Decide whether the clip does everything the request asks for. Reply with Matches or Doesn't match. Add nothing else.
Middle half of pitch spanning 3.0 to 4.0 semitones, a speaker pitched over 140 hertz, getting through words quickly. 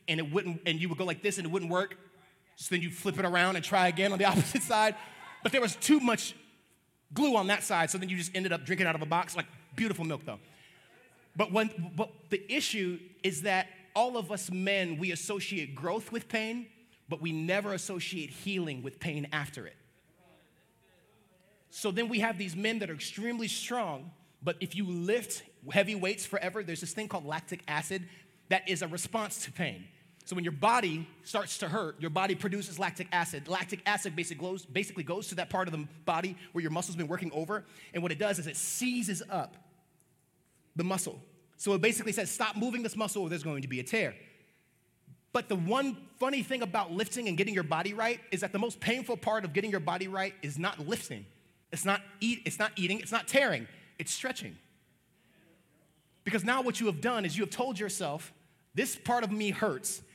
Matches